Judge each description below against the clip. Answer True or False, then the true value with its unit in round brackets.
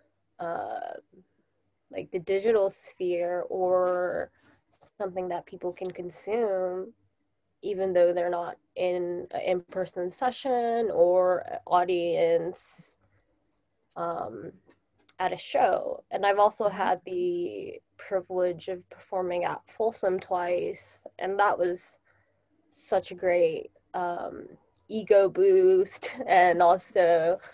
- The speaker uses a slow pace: True (105 wpm)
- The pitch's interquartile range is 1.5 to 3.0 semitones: False (3.9 semitones)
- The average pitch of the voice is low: False (185 Hz)